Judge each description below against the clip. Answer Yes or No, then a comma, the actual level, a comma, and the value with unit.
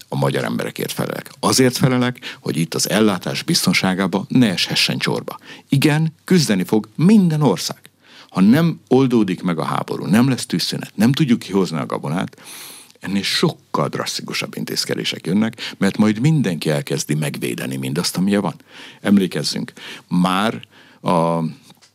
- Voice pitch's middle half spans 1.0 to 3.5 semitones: No, wide, 7.4 semitones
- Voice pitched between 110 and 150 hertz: No, low, 100 Hz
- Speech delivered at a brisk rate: No, average, 135 wpm